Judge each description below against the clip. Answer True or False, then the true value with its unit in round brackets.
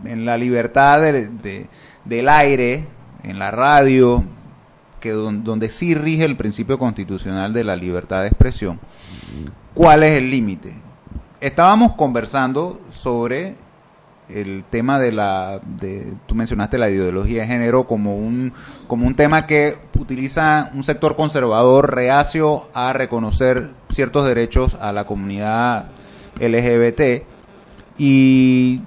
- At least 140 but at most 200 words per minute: False (125 wpm)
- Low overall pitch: True (125 Hz)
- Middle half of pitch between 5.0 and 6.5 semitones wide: False (4.1 semitones)